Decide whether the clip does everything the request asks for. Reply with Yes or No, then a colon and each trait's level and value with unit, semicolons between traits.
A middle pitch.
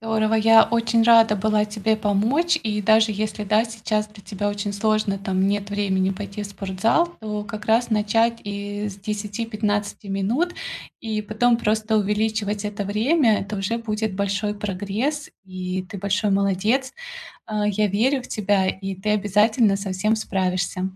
No: high, 210 Hz